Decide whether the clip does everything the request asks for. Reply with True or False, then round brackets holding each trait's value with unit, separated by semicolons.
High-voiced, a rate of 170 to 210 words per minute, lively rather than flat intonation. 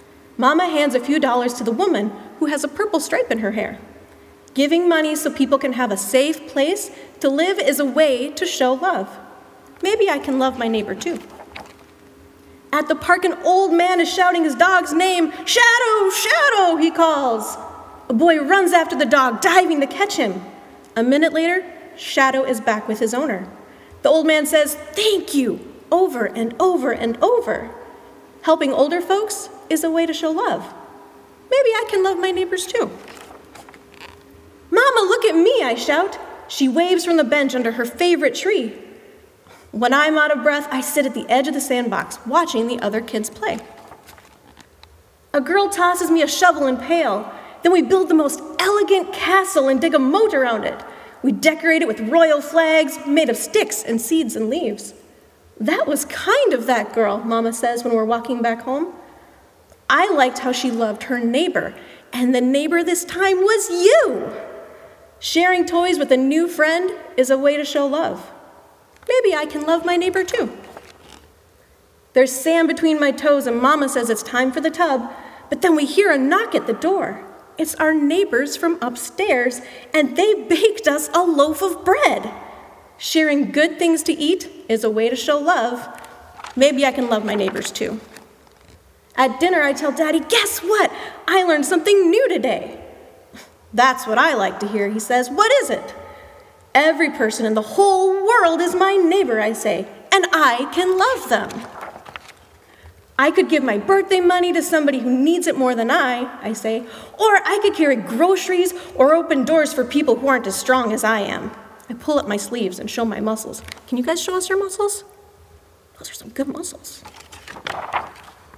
True (305 Hz; 180 wpm; 5.9 semitones)